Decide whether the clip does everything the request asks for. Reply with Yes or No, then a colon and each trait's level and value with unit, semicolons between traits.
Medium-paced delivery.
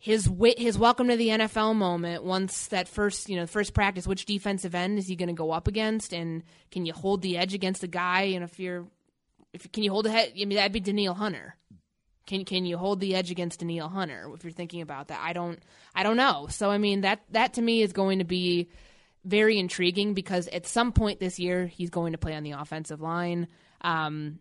No: fast, 230 wpm